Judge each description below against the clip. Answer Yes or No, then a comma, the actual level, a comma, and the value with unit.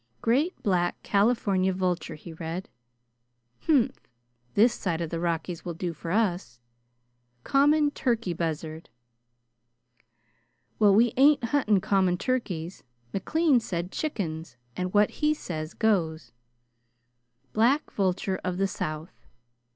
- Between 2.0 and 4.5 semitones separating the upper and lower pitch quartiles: No, wide, 5.5 semitones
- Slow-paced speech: Yes, slow, 110 wpm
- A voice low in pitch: No, high, 190 Hz